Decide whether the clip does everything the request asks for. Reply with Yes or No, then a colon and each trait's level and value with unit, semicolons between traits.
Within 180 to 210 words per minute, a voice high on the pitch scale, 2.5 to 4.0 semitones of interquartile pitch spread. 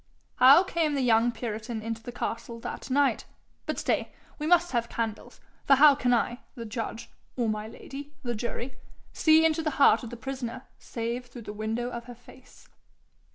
Yes: average, 185 wpm; high, 245 Hz; average, 3.1 semitones